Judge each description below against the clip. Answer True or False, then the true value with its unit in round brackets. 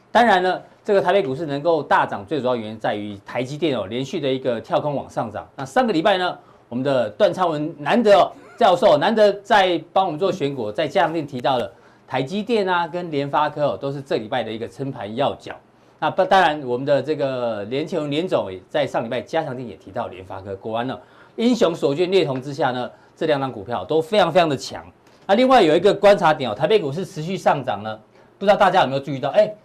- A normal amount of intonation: False (6.5 semitones)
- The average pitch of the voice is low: False (150 Hz)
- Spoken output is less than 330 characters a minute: False (345 characters per minute)